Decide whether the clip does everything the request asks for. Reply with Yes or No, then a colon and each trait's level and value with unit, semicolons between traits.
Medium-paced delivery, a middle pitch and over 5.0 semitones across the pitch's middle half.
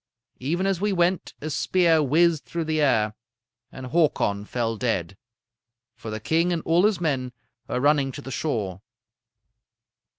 Yes: average, 155 wpm; medium, 150 Hz; wide, 5.6 semitones